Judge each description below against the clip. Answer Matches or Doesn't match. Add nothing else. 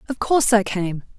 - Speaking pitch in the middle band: Doesn't match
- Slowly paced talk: Doesn't match